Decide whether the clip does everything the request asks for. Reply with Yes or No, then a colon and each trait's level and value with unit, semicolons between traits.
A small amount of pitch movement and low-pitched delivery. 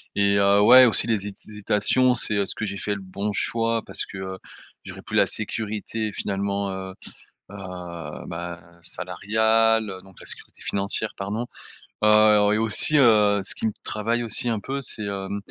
Yes: narrow, 2.2 semitones; low, 105 Hz